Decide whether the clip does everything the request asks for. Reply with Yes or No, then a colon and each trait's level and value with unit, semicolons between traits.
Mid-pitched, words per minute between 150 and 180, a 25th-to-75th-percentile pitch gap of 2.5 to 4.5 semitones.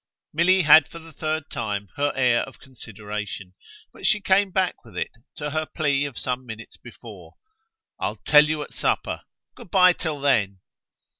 No: medium, 145 Hz; average, 170 wpm; wide, 5.4 semitones